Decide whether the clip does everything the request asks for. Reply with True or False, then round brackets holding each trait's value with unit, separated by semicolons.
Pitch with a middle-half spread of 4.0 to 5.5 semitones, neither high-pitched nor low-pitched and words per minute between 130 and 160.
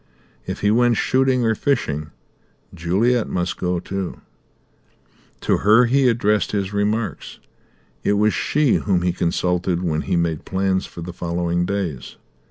False (4.3 semitones; 95 Hz; 145 wpm)